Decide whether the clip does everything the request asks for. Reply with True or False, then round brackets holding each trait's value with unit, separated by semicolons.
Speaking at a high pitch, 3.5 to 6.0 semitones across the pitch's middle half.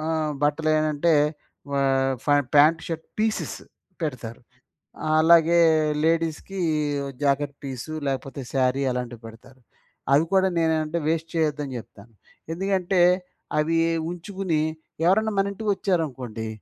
False (155 Hz; 4.0 semitones)